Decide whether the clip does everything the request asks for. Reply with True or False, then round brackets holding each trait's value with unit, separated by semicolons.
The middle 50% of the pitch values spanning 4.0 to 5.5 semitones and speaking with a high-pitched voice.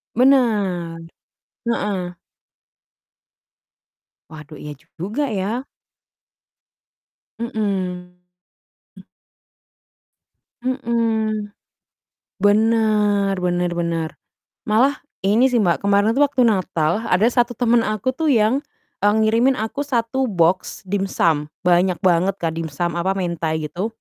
True (4.5 semitones; 205 Hz)